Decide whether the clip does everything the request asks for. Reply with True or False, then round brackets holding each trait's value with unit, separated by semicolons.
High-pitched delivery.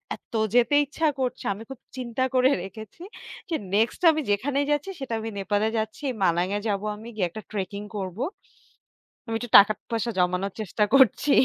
True (225 Hz)